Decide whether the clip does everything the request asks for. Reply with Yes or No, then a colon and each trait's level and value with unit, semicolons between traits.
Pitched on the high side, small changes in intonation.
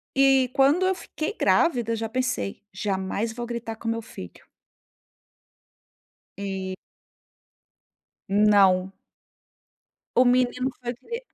No: high, 230 Hz; average, 4.2 semitones